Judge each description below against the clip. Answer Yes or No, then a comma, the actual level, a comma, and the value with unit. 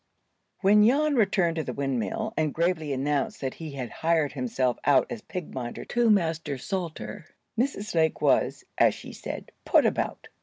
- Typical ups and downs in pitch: No, wide, 6.8 semitones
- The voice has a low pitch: No, medium, 165 Hz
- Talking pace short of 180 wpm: Yes, average, 165 wpm